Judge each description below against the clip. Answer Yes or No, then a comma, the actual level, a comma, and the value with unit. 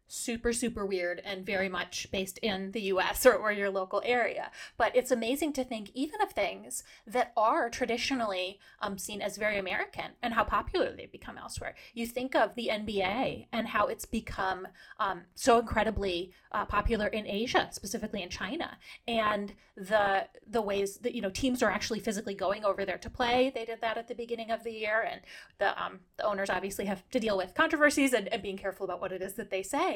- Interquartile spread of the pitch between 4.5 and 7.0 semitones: No, average, 3.3 semitones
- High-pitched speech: Yes, high, 220 Hz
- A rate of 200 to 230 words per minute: Yes, fast, 205 wpm